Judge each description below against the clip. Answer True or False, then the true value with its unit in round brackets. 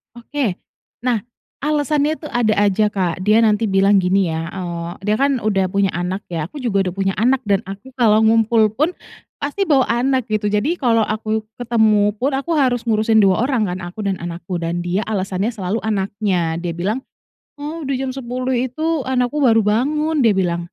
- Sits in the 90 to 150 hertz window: False (215 Hz)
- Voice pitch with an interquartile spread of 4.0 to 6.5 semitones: True (4.9 semitones)